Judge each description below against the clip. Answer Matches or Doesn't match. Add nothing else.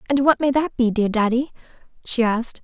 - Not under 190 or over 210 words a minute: Matches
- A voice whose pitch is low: Doesn't match